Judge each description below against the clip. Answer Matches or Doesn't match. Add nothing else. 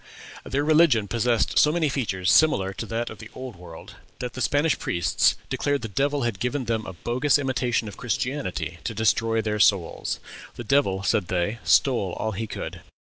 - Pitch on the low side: Matches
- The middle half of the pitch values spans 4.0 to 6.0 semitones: Matches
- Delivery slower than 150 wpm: Doesn't match